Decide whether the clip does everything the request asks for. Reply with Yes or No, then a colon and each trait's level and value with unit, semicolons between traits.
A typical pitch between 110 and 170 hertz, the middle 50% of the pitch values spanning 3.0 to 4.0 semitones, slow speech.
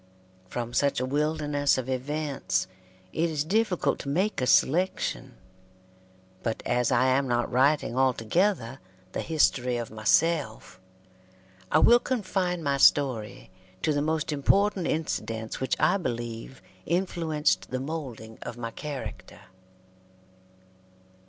No: medium, 140 Hz; average, 4.8 semitones; slow, 120 wpm